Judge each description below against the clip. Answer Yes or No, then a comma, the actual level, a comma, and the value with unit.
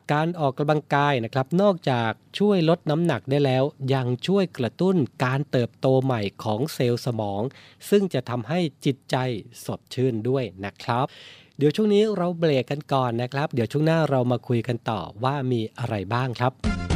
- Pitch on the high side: No, low, 130 Hz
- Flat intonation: No, average, 3.9 semitones